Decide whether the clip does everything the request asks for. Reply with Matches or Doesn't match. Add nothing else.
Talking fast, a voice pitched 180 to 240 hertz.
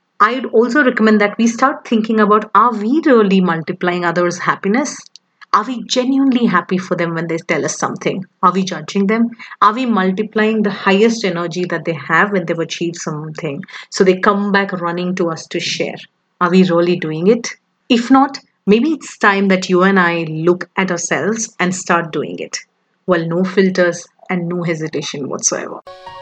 Doesn't match